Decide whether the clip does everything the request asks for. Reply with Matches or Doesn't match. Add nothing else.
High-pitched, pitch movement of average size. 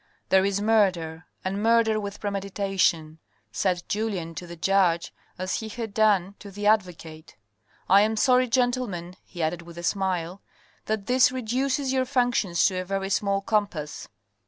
Matches